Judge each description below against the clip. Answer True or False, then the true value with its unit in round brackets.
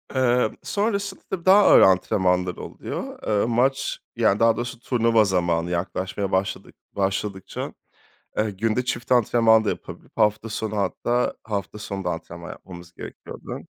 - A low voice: True (105 Hz)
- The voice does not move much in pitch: False (4.2 semitones)